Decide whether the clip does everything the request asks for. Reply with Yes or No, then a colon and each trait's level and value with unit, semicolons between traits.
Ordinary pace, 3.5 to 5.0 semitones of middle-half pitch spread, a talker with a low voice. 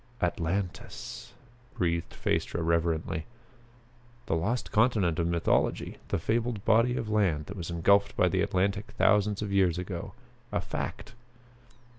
No: slow, 130 wpm; average, 3.8 semitones; very low, 95 Hz